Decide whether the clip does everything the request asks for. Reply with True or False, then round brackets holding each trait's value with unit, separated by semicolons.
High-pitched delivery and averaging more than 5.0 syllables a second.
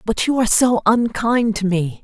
False (215 Hz; 4.9 syllables/s)